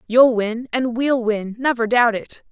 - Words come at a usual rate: Yes, average, 165 wpm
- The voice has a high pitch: Yes, high, 235 Hz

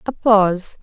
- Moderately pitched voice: No, high, 205 Hz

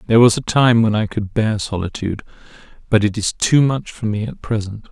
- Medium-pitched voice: No, low, 110 Hz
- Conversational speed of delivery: No, fast, 220 wpm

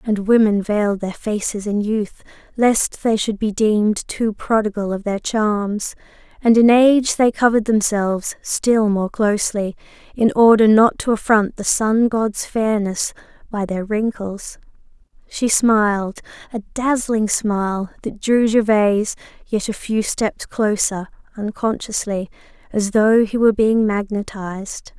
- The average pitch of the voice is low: No, high, 215 Hz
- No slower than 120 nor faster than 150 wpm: Yes, average, 140 wpm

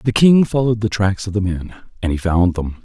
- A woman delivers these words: No, male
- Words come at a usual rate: No, fast, 255 wpm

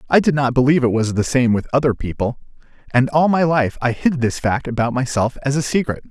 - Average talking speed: No, fast, 235 wpm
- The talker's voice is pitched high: No, low, 130 Hz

